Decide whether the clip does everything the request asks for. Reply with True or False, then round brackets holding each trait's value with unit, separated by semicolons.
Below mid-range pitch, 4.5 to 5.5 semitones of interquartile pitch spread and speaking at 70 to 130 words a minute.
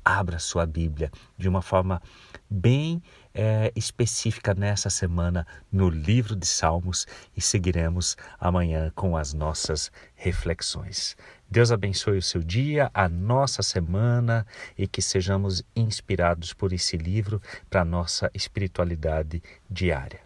False (95 Hz; 3.7 semitones; 125 wpm)